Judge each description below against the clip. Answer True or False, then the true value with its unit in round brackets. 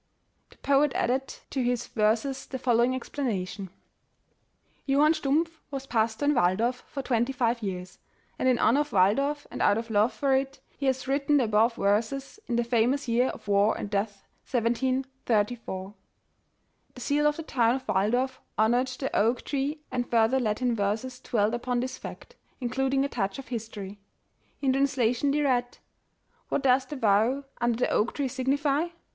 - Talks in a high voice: True (250 Hz)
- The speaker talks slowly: False (175 wpm)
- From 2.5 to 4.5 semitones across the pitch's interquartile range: True (3.4 semitones)